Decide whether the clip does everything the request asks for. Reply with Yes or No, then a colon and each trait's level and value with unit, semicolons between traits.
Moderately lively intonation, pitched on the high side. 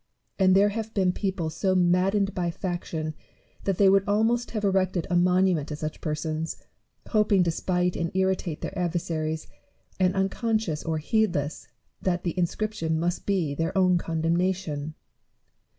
No: average, 3.0 semitones; medium, 180 Hz